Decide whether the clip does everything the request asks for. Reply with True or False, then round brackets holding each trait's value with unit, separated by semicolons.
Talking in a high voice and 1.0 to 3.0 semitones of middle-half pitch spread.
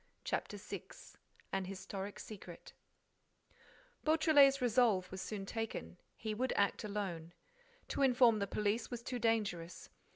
False (215 Hz; 4.1 semitones)